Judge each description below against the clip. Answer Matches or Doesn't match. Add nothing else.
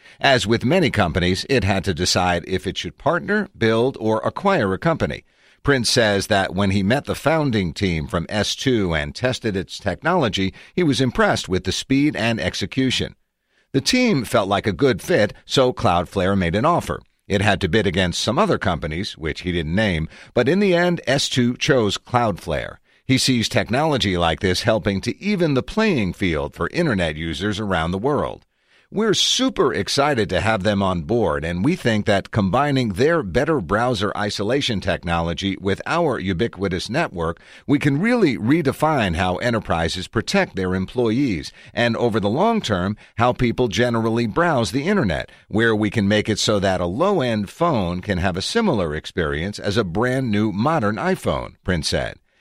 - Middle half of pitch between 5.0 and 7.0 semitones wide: Matches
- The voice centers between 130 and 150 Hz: Doesn't match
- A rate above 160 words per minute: Matches